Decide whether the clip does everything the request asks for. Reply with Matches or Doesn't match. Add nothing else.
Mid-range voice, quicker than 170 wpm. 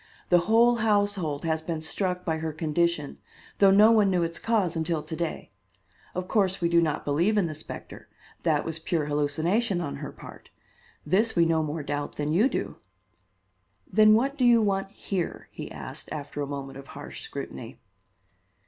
Matches